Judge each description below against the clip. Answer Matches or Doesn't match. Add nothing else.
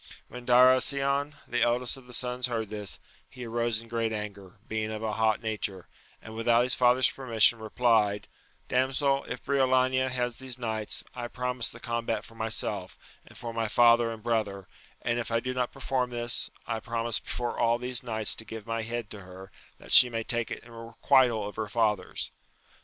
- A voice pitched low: Matches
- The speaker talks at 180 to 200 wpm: Matches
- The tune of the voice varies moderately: Doesn't match